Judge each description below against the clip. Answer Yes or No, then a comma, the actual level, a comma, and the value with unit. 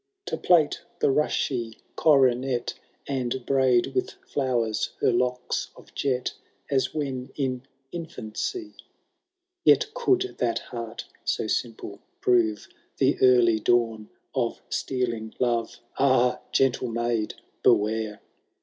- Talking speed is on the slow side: Yes, slow, 115 wpm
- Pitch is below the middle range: Yes, low, 125 Hz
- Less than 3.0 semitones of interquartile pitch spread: Yes, narrow, 2.6 semitones